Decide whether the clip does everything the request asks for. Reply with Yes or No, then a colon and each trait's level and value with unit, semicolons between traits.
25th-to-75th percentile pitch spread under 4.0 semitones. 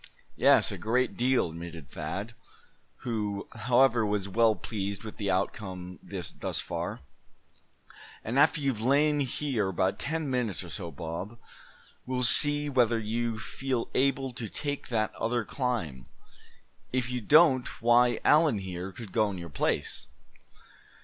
No: average, 4.8 semitones